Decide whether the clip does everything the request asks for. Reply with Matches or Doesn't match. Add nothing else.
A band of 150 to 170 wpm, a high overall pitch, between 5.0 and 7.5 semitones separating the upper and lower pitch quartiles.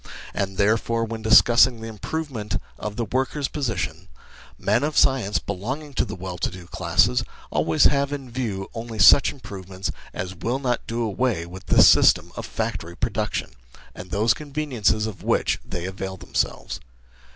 Doesn't match